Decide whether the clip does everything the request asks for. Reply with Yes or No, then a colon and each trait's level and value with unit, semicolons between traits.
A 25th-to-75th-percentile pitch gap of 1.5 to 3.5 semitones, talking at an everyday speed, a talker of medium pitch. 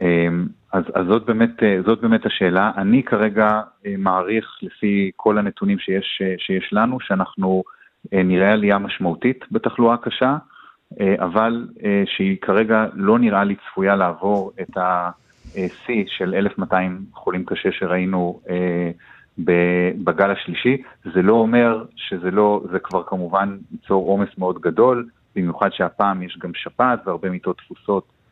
No: average, 3.1 semitones; average, 125 wpm; low, 100 Hz